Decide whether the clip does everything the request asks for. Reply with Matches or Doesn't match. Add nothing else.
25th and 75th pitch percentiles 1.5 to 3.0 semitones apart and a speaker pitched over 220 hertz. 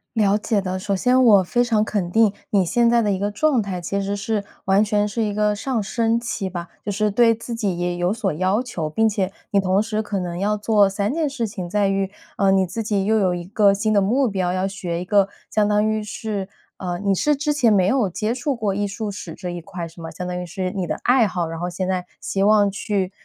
Doesn't match